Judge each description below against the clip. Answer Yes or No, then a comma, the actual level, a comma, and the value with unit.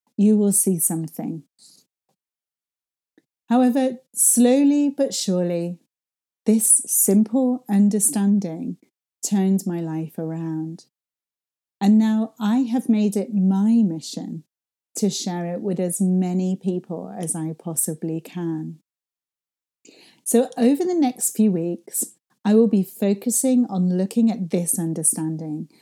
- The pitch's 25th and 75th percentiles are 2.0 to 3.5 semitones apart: No, average, 4.8 semitones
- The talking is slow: Yes, slow, 115 wpm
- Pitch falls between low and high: No, high, 195 Hz